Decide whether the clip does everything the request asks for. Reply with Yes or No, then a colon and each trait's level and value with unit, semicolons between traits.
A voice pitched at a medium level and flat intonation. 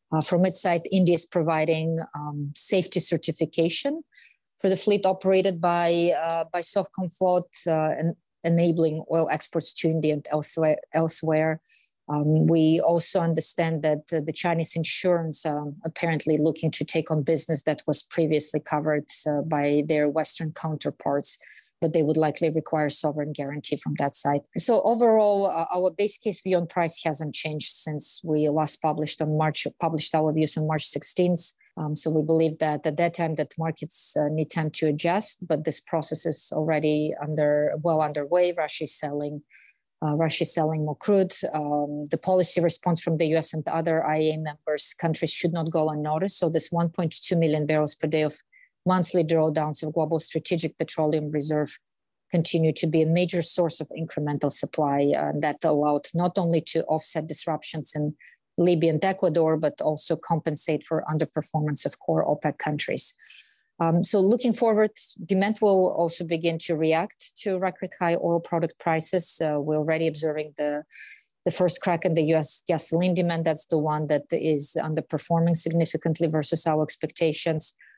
Yes: medium, 160 Hz; narrow, 1.9 semitones